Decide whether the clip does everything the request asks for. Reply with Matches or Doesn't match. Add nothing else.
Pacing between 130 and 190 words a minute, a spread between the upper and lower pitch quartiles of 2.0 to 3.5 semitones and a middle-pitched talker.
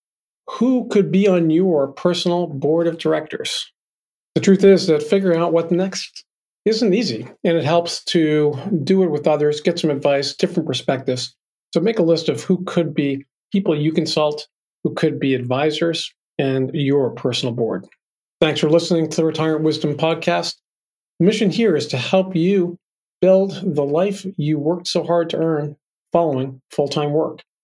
Matches